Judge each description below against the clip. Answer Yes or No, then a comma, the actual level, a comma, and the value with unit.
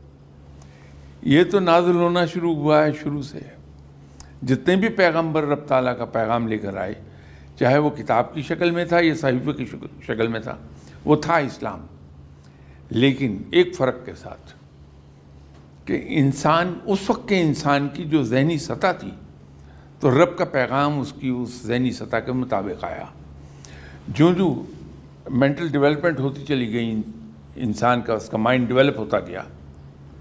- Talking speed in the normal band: Yes, average, 155 wpm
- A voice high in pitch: No, low, 125 Hz